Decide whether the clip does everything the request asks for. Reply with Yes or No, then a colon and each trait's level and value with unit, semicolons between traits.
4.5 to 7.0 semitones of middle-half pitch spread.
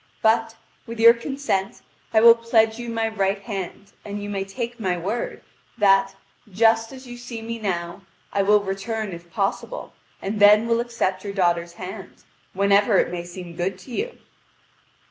No: average, 3.1 semitones